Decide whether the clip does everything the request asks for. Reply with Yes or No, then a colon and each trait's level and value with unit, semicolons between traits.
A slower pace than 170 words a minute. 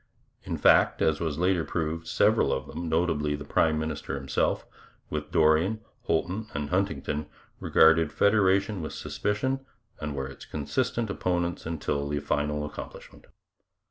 Yes: average, 140 wpm